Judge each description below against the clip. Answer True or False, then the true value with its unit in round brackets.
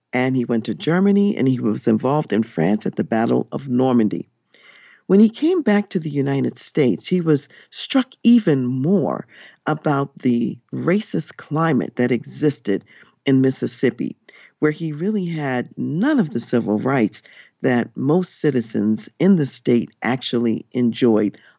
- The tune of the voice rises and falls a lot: True (6.7 semitones)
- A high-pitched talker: False (140 Hz)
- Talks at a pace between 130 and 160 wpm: True (150 wpm)